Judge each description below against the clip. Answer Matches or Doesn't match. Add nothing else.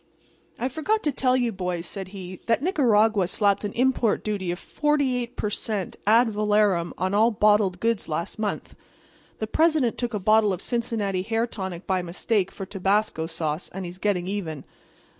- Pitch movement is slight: Doesn't match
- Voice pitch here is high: Matches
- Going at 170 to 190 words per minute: Matches